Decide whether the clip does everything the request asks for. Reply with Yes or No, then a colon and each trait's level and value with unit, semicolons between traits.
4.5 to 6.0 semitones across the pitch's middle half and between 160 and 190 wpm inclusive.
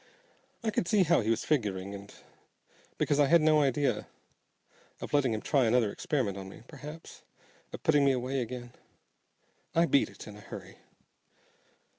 Yes: wide, 5.4 semitones; average, 165 wpm